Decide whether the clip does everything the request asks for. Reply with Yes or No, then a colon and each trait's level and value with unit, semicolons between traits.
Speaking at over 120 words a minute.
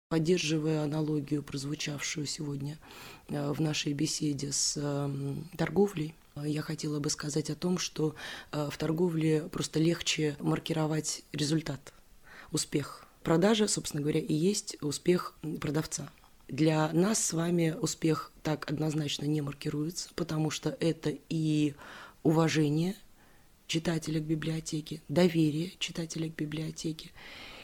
No: slow, 110 wpm